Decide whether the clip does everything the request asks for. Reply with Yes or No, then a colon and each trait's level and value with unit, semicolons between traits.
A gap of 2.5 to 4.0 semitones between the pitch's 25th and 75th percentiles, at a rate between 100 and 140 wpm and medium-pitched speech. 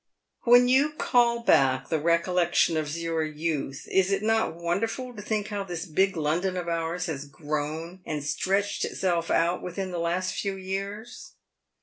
No: average, 3.6 semitones; average, 160 wpm; medium, 180 Hz